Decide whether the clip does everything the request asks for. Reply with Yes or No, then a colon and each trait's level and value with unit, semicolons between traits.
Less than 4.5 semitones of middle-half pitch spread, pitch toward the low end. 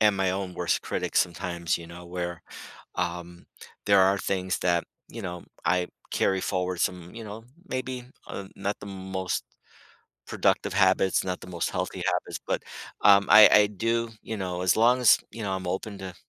Yes: narrow, 2.4 semitones; very low, 95 Hz